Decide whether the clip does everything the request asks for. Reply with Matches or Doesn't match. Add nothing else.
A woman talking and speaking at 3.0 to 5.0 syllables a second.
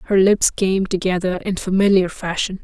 Matches